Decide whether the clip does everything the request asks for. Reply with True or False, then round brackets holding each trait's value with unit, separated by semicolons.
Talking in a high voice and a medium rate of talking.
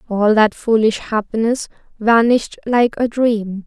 False (225 Hz; 130 wpm)